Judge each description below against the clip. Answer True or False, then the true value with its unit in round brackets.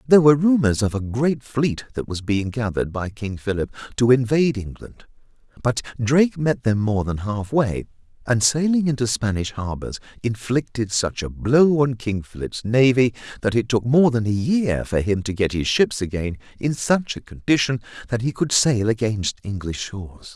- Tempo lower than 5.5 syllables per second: True (4.9 syllables/s)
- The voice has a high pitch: False (115 Hz)